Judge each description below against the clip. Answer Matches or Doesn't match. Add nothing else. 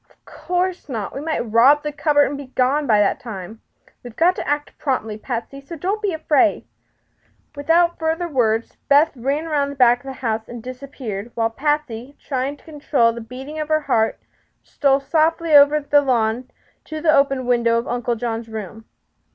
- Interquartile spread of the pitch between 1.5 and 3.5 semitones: Doesn't match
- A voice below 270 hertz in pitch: Doesn't match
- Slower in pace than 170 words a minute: Doesn't match